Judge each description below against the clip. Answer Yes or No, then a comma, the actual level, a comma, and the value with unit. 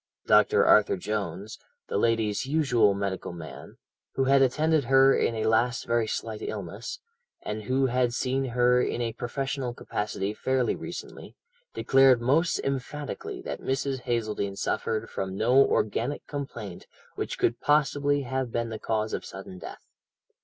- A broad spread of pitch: No, average, 3.8 semitones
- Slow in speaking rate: No, average, 145 wpm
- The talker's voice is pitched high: No, low, 120 Hz